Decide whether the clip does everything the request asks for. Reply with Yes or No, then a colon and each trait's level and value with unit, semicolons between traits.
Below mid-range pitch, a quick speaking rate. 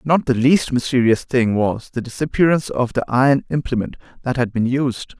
No: low, 130 Hz; average, 185 wpm